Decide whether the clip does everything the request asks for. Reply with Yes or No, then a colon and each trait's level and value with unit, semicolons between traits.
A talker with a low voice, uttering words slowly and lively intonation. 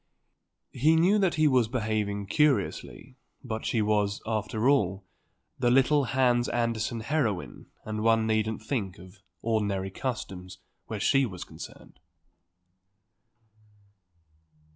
No: low, 110 Hz; slow, 115 wpm; average, 3.9 semitones